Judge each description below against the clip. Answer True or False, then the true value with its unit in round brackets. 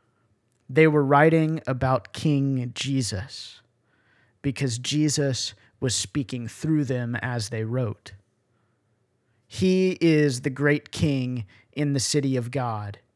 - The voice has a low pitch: True (125 Hz)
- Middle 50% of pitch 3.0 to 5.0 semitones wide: True (3.9 semitones)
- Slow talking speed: True (115 wpm)